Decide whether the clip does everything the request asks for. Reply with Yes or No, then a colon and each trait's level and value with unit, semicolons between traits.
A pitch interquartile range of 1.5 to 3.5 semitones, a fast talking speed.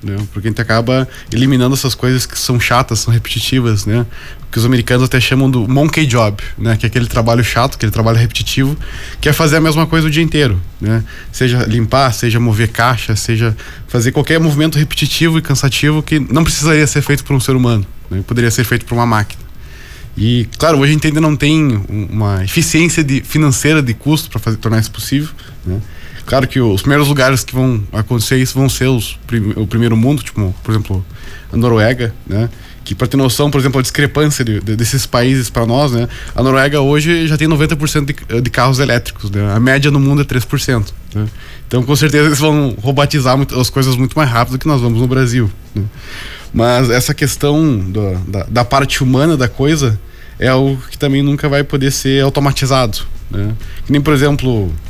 No: average, 4.0 semitones; fast, 205 wpm